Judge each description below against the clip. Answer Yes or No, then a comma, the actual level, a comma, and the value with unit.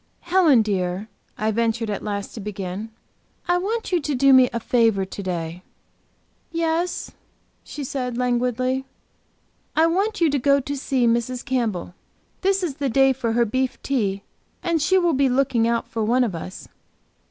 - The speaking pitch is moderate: No, very high, 250 Hz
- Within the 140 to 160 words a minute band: No, average, 170 wpm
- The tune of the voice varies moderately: Yes, average, 4.6 semitones